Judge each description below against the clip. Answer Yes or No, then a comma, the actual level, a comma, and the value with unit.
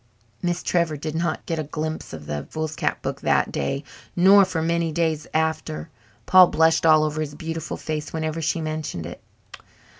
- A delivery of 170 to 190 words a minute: Yes, average, 175 wpm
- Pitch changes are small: Yes, narrow, 1.3 semitones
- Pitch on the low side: No, medium, 160 Hz